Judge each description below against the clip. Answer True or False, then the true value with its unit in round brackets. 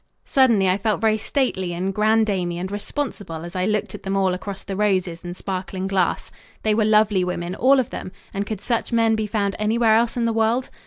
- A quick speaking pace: True (215 wpm)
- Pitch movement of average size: True (3.0 semitones)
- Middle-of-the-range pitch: False (205 Hz)